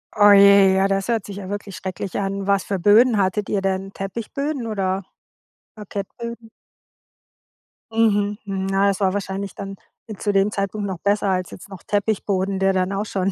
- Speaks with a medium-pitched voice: No, high, 200 Hz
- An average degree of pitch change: No, narrow, 1.2 semitones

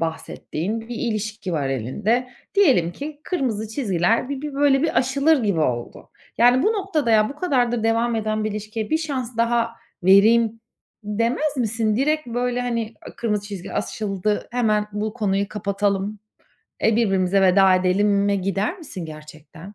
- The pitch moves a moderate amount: Yes, average, 3.8 semitones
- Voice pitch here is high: Yes, high, 220 Hz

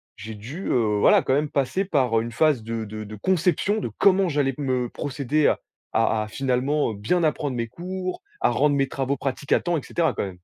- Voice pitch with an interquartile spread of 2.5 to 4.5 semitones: No, wide, 5.4 semitones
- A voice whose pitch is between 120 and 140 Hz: Yes, low, 135 Hz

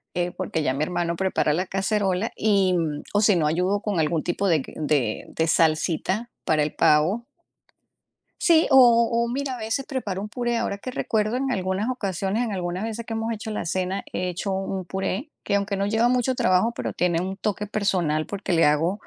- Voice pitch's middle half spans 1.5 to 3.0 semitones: No, average, 4.3 semitones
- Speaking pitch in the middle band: No, high, 195 Hz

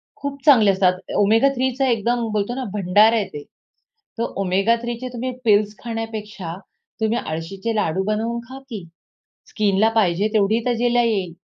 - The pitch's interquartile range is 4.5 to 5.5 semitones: No, average, 3.2 semitones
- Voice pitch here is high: Yes, high, 220 Hz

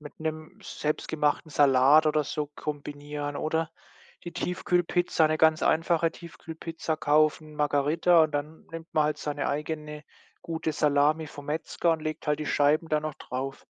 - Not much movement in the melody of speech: Yes, narrow, 1.4 semitones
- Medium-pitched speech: Yes, medium, 155 Hz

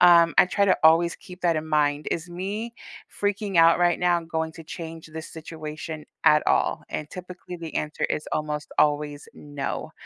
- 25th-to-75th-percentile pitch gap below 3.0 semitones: Yes, narrow, 2.5 semitones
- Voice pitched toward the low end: No, medium, 165 Hz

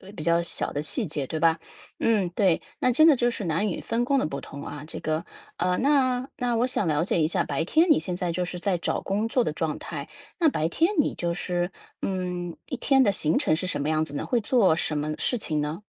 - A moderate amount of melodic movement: No, wide, 7.0 semitones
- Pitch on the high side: No, medium, 180 Hz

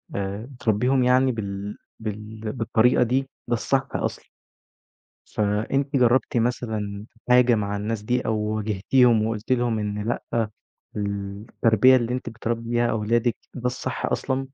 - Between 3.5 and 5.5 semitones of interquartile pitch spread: No, average, 2.7 semitones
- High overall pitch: No, low, 115 Hz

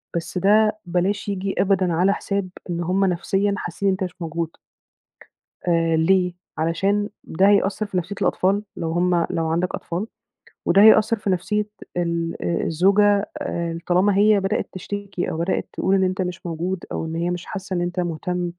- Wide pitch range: No, average, 2.7 semitones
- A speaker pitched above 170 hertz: Yes, medium, 185 Hz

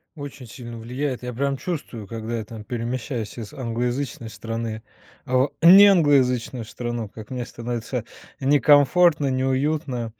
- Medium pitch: No, low, 125 Hz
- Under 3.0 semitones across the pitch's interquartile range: No, average, 3.4 semitones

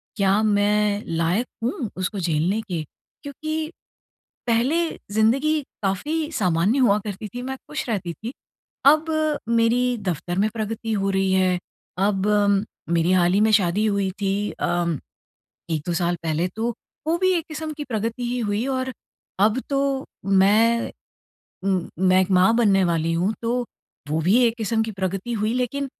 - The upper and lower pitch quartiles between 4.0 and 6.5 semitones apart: Yes, average, 4.4 semitones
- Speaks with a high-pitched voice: Yes, high, 210 Hz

